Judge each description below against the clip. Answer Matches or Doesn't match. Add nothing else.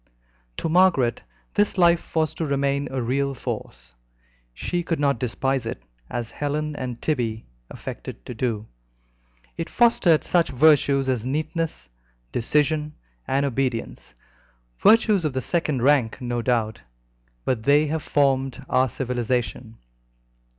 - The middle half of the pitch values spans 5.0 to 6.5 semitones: Doesn't match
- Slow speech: Matches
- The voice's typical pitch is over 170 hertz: Doesn't match